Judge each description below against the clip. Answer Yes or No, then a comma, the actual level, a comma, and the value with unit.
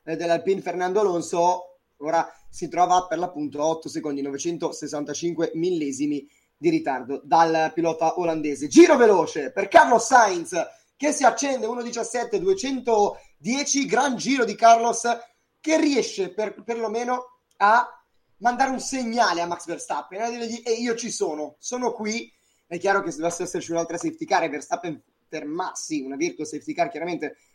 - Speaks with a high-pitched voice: Yes, high, 210 Hz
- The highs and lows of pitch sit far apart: Yes, wide, 7.0 semitones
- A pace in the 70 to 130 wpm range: No, average, 145 wpm